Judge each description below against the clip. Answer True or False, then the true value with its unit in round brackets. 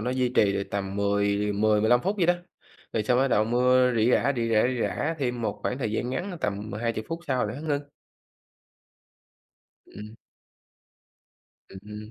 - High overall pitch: False (115 Hz)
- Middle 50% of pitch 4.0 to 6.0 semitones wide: False (3.5 semitones)